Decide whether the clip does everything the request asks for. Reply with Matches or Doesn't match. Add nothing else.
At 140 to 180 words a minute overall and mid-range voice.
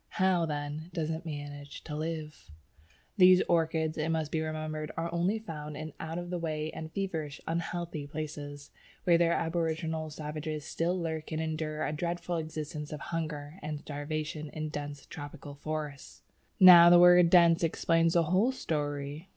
Matches